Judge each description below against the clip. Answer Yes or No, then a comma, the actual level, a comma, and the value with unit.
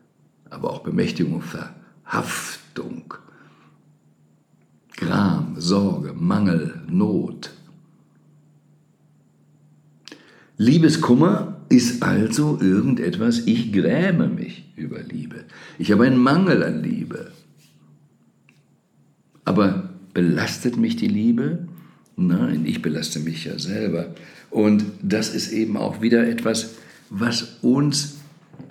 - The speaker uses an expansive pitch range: Yes, wide, 9.0 semitones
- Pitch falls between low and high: No, low, 130 Hz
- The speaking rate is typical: No, slow, 90 wpm